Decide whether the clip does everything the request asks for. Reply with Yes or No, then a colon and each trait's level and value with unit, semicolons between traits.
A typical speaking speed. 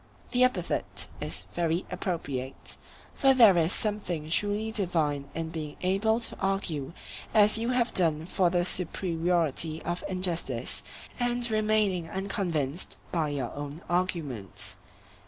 No: slow, 125 wpm